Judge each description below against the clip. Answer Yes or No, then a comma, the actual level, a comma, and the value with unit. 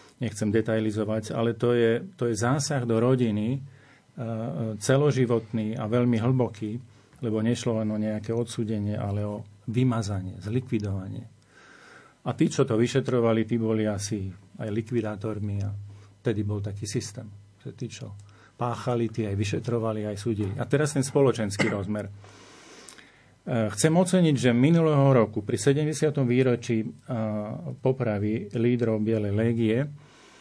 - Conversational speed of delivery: Yes, average, 135 wpm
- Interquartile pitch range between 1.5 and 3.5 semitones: Yes, average, 2.7 semitones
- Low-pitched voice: Yes, low, 115 Hz